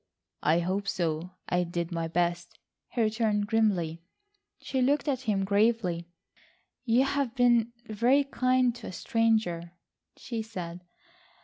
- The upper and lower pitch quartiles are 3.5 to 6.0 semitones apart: Yes, wide, 5.5 semitones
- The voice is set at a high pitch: Yes, high, 210 Hz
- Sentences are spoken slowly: Yes, slow, 130 wpm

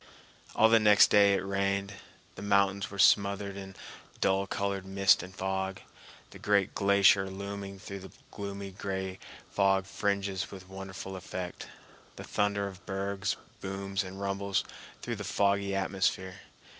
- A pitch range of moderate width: No, narrow, 0.7 semitones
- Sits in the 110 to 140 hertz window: No, low, 100 Hz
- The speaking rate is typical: Yes, average, 145 wpm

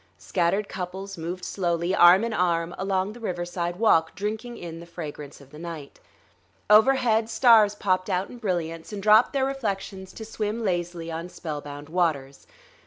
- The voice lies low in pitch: No, medium, 185 Hz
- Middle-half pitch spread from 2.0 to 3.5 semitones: No, average, 3.9 semitones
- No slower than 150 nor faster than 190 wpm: Yes, average, 160 wpm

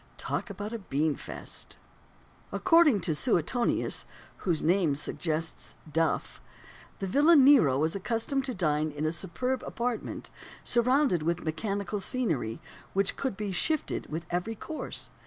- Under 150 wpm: Yes, slow, 135 wpm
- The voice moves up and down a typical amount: No, wide, 7.6 semitones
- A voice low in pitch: No, high, 195 Hz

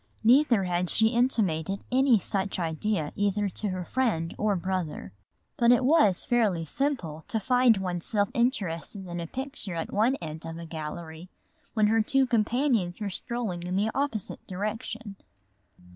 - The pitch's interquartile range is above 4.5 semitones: Yes, average, 5.3 semitones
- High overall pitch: Yes, high, 205 Hz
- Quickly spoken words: No, average, 160 wpm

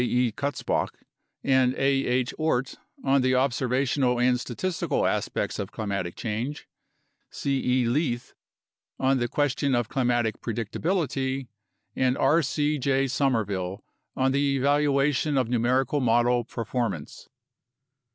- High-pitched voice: No, low, 130 Hz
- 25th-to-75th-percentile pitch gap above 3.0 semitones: No, narrow, 2.4 semitones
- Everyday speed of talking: No, slow, 125 wpm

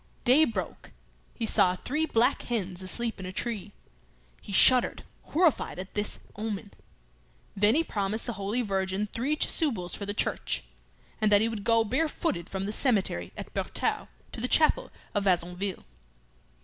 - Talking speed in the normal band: Yes, average, 160 wpm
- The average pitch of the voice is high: Yes, high, 210 Hz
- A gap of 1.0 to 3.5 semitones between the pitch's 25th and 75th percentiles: No, average, 3.9 semitones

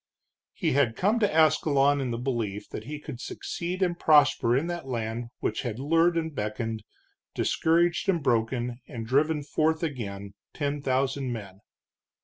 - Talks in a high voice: No, low, 135 Hz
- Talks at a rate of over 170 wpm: No, average, 155 wpm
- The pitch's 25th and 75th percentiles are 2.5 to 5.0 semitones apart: No, wide, 5.4 semitones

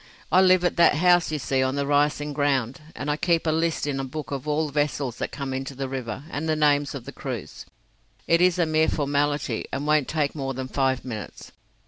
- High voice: No, medium, 145 Hz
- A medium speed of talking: No, fast, 225 wpm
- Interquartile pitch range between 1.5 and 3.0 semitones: Yes, narrow, 2.6 semitones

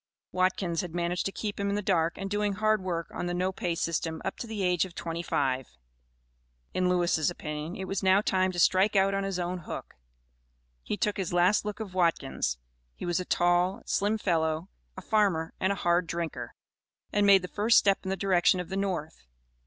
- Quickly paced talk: Yes, fast, 210 wpm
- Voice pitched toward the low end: No, medium, 185 Hz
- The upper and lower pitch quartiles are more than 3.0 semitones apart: No, narrow, 2.4 semitones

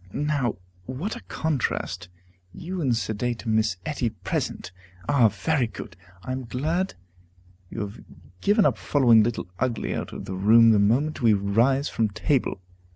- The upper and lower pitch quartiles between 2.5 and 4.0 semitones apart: No, average, 5.0 semitones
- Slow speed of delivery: No, average, 155 wpm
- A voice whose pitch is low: Yes, low, 120 Hz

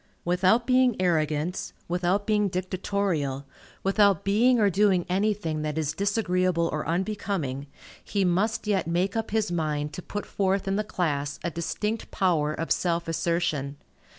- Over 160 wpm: No, average, 150 wpm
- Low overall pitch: No, medium, 180 Hz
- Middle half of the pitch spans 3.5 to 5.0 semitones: Yes, average, 4.0 semitones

